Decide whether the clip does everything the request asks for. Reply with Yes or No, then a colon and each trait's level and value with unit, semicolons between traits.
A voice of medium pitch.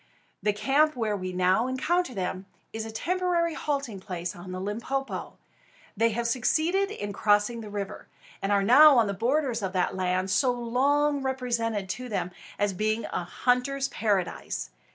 No: high, 230 Hz